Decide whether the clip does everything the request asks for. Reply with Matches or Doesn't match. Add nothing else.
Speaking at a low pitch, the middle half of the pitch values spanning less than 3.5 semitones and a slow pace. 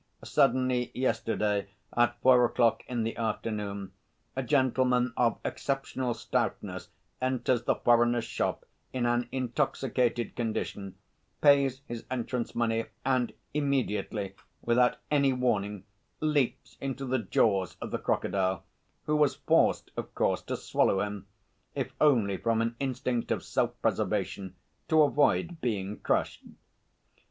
Matches